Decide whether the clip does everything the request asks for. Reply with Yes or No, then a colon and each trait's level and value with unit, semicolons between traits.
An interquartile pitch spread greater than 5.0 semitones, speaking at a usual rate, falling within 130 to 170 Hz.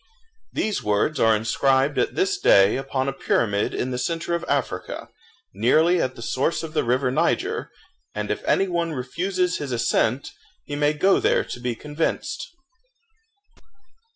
Yes: wide, 5.4 semitones; average, 155 wpm; medium, 140 Hz